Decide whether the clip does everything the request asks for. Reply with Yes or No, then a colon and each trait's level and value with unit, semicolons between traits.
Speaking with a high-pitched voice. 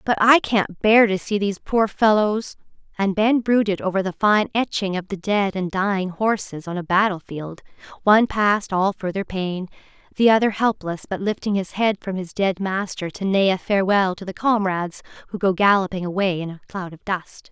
Yes: high, 195 Hz